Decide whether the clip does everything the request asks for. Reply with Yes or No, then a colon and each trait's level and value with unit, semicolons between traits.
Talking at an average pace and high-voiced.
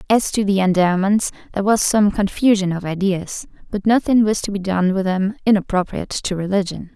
Yes: average, 180 wpm; high, 195 Hz